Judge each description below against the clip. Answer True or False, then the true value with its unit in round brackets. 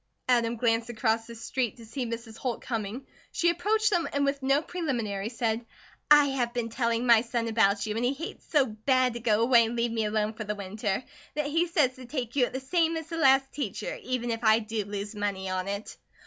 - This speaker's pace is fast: True (230 wpm)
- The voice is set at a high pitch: True (235 Hz)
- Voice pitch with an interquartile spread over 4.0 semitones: False (3.4 semitones)